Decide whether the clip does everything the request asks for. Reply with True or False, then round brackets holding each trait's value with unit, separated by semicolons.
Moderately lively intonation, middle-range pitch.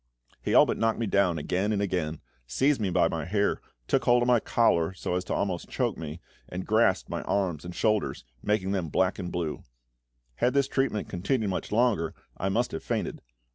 False (4.1 semitones; 95 Hz)